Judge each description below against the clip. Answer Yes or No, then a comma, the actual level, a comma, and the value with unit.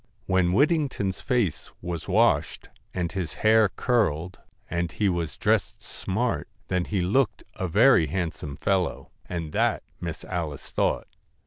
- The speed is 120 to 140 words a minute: Yes, slow, 135 wpm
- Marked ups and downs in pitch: No, average, 4.1 semitones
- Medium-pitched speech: No, very low, 95 Hz